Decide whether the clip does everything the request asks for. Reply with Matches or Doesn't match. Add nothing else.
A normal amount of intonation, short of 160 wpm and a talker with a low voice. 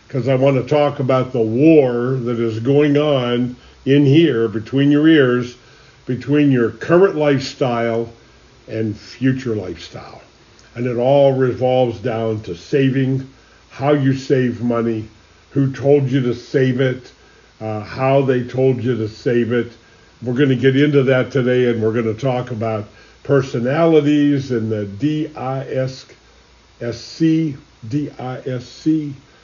Matches